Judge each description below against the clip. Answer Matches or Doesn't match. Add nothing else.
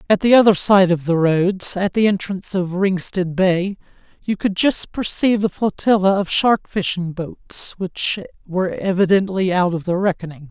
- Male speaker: Matches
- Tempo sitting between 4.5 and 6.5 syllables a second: Matches